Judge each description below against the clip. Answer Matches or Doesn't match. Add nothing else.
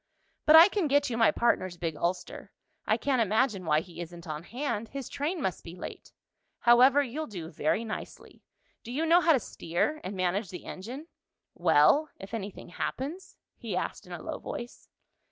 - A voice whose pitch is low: Doesn't match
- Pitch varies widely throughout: Matches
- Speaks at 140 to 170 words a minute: Doesn't match